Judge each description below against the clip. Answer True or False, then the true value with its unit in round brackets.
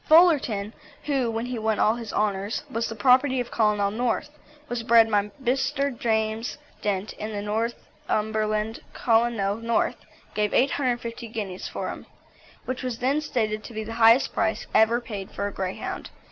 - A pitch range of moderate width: False (2.3 semitones)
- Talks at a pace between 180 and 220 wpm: False (160 wpm)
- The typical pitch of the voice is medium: False (225 Hz)